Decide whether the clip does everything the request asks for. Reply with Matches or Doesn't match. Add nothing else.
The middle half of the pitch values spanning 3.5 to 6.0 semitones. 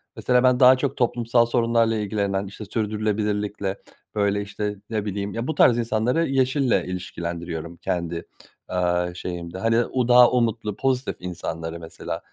Matches